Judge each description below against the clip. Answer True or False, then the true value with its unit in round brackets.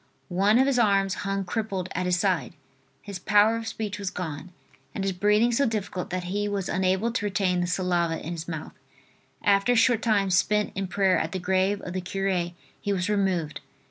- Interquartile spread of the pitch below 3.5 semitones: True (2.4 semitones)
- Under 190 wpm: False (205 wpm)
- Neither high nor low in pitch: False (195 Hz)